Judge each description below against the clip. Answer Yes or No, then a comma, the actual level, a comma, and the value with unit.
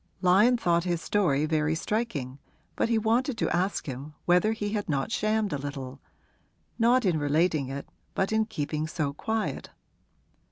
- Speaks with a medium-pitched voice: Yes, medium, 175 Hz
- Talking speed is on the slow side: No, average, 160 wpm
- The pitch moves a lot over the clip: Yes, wide, 6.8 semitones